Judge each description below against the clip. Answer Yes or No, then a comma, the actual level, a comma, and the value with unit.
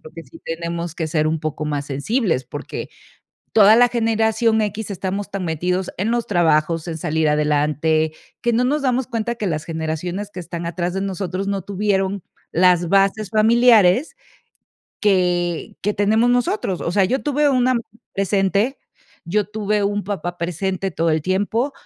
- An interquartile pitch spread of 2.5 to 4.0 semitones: No, average, 4.5 semitones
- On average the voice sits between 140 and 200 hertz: Yes, high, 190 Hz